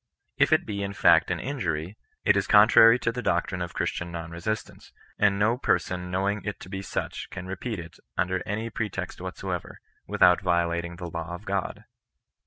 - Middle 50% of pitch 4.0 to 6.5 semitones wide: No, average, 3.2 semitones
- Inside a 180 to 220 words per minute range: Yes, average, 190 wpm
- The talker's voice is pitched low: Yes, very low, 95 Hz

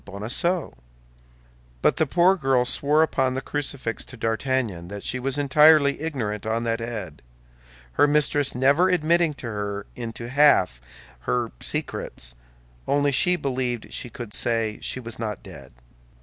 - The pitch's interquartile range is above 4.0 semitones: Yes, average, 5.1 semitones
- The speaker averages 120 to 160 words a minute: Yes, slow, 135 wpm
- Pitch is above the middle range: No, low, 125 Hz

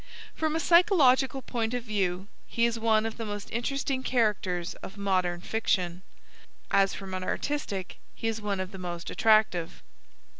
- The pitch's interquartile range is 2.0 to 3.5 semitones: No, average, 4.5 semitones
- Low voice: No, high, 215 Hz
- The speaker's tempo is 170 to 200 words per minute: No, average, 160 wpm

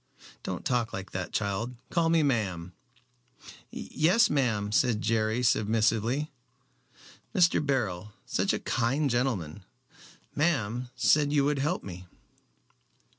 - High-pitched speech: No, low, 120 Hz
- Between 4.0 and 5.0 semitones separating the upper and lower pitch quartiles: No, wide, 5.6 semitones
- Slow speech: Yes, slow, 115 wpm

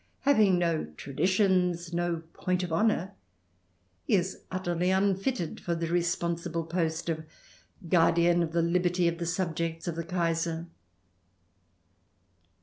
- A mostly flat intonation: Yes, narrow, 1.5 semitones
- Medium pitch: Yes, medium, 170 Hz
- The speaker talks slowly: Yes, slow, 125 wpm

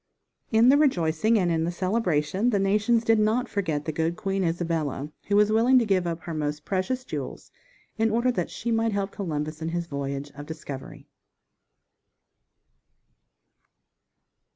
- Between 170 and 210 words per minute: No, average, 160 wpm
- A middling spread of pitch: No, wide, 5.8 semitones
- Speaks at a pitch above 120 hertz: Yes, medium, 185 Hz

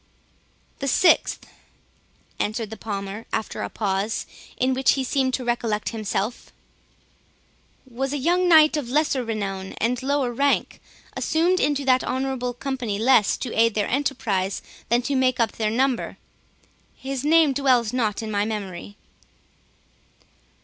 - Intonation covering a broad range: No, average, 4.0 semitones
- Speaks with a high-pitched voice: Yes, very high, 250 Hz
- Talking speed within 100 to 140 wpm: Yes, slow, 135 wpm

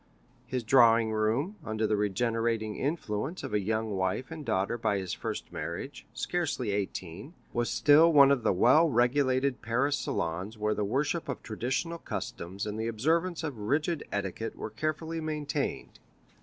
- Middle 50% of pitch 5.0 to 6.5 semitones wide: Yes, wide, 5.5 semitones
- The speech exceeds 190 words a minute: No, average, 160 wpm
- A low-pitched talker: Yes, low, 120 Hz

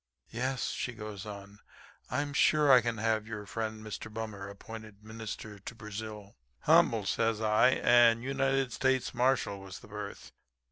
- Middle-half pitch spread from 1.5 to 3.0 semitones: Yes, average, 2.7 semitones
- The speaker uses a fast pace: No, average, 155 wpm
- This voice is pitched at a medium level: No, low, 110 Hz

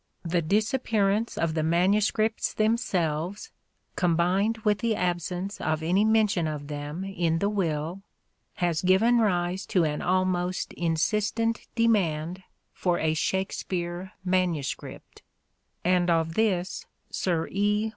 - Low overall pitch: No, medium, 185 Hz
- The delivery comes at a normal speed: No, slow, 125 wpm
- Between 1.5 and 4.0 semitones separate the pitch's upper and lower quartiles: Yes, average, 3.7 semitones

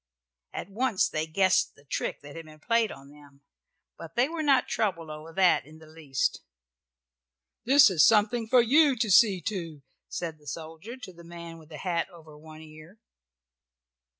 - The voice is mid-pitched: Yes, medium, 170 Hz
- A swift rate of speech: No, average, 180 wpm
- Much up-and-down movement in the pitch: Yes, wide, 5.9 semitones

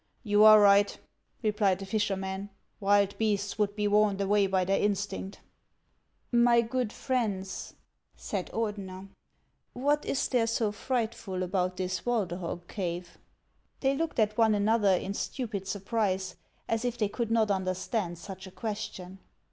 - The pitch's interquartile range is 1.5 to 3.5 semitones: Yes, average, 2.8 semitones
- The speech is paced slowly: No, average, 155 wpm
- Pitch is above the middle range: Yes, high, 205 Hz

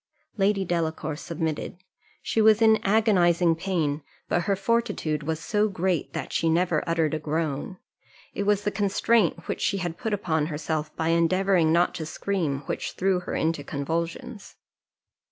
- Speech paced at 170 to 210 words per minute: No, average, 155 wpm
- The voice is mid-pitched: Yes, medium, 170 Hz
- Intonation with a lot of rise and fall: No, average, 3.8 semitones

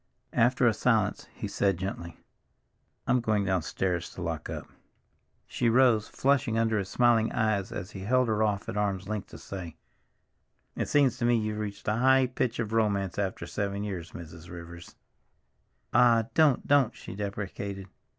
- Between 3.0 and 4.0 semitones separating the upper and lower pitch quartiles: Yes, average, 3.5 semitones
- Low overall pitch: Yes, low, 105 Hz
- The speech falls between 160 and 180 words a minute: Yes, average, 170 wpm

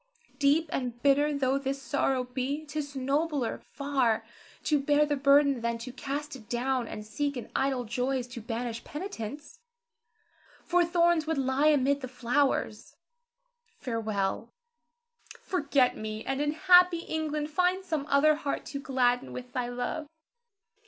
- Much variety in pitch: No, average, 3.2 semitones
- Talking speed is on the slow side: No, average, 145 wpm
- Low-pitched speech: No, very high, 275 Hz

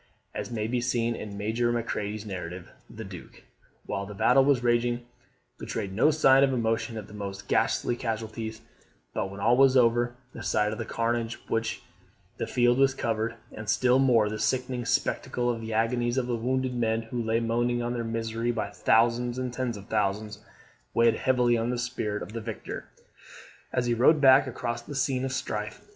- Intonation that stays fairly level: Yes, narrow, 1.9 semitones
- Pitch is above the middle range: No, low, 115 Hz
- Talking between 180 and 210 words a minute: Yes, average, 190 wpm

